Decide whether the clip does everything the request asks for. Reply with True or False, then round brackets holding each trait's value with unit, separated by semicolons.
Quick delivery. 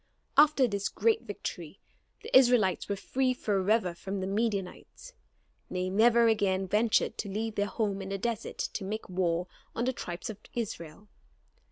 False (160 wpm)